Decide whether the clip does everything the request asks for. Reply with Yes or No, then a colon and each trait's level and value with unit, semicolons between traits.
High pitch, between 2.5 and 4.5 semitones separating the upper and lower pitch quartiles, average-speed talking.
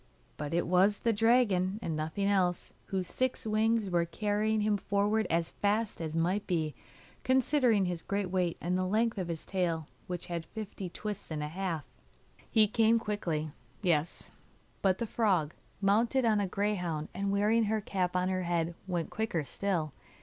Yes: high, 195 Hz; average, 3.7 semitones; average, 170 wpm